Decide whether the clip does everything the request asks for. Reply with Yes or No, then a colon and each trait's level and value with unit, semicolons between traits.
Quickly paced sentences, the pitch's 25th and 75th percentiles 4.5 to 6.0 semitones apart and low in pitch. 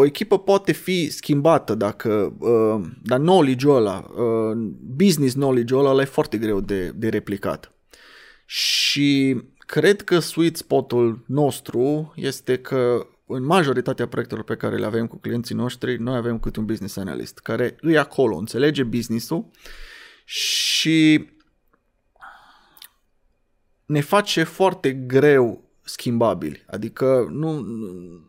No: average, 120 wpm; wide, 5.5 semitones; low, 130 Hz